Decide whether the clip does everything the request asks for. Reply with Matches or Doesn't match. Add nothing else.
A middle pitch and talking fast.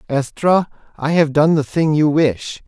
Doesn't match